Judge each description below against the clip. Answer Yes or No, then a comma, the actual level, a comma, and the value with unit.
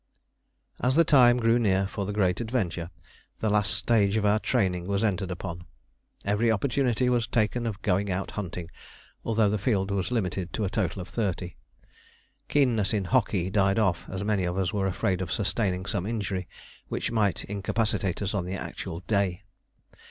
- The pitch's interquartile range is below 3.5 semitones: Yes, average, 3.1 semitones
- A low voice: Yes, low, 100 Hz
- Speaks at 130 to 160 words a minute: No, average, 175 wpm